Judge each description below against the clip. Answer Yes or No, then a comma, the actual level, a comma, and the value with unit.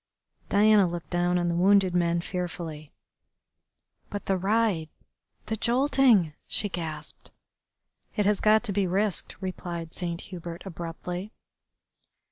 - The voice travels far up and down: No, average, 3.2 semitones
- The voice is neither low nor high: Yes, medium, 180 Hz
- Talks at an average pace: No, slow, 120 wpm